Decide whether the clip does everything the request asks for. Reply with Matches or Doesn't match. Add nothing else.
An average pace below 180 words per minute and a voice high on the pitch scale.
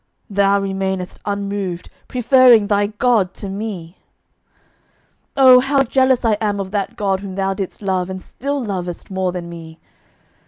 Matches